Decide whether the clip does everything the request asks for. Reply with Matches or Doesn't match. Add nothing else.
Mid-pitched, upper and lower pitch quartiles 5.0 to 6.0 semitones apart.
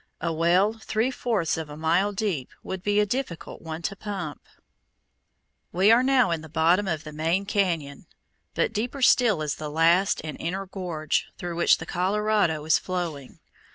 Doesn't match